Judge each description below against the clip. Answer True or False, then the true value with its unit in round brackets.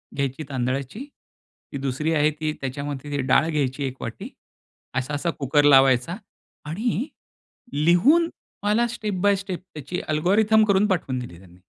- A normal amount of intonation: False (6.5 semitones)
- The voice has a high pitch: False (150 Hz)